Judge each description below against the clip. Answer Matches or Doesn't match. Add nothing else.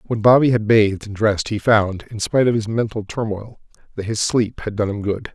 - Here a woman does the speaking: Doesn't match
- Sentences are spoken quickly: Matches